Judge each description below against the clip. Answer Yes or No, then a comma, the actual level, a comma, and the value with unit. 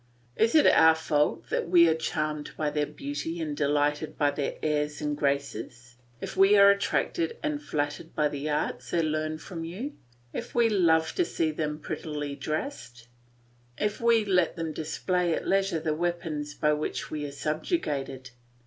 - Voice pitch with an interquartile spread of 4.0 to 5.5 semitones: No, average, 3.5 semitones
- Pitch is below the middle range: No, medium, 155 Hz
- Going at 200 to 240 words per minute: No, average, 170 wpm